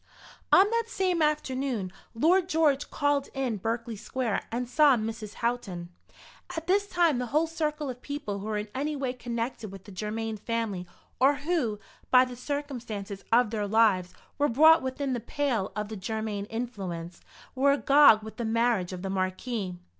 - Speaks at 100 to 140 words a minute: No, average, 170 wpm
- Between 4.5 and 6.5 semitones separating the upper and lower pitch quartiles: Yes, average, 5.3 semitones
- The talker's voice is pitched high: Yes, high, 240 Hz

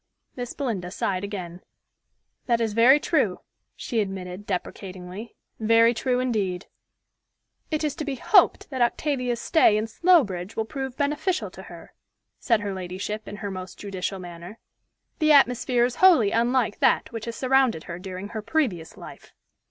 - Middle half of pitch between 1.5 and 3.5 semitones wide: No, average, 5.1 semitones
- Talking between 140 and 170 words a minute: Yes, average, 155 wpm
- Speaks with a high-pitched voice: Yes, high, 225 Hz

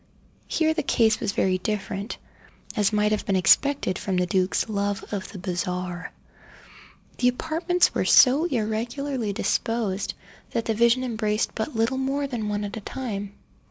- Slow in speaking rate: No, average, 160 wpm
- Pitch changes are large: No, average, 4.2 semitones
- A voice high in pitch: Yes, high, 215 Hz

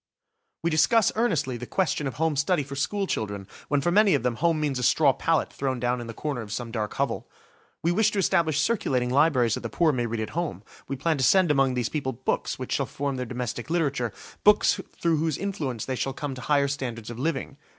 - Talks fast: Yes, fast, 230 wpm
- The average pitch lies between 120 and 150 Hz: Yes, medium, 140 Hz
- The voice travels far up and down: No, average, 5.0 semitones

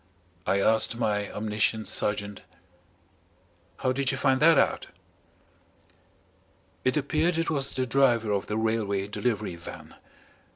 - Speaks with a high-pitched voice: No, low, 115 Hz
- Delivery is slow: Yes, slow, 125 wpm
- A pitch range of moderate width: Yes, average, 4.6 semitones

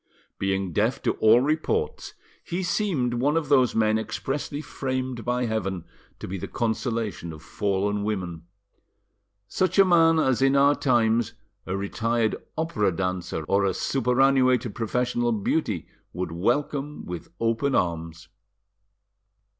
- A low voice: Yes, low, 115 Hz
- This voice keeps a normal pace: No, slow, 130 wpm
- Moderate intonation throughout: No, wide, 5.8 semitones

